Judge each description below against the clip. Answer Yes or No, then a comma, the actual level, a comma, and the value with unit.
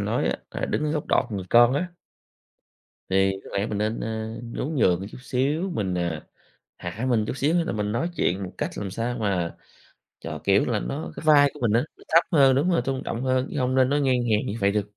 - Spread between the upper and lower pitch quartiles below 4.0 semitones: No, average, 5.1 semitones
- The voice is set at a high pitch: No, low, 120 Hz